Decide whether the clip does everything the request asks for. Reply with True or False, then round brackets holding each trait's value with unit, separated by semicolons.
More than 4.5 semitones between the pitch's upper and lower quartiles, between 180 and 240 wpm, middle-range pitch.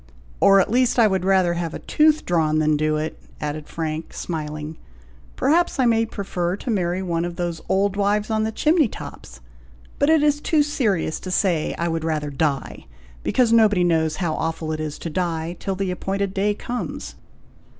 True (5.2 semitones; 190 wpm; 180 Hz)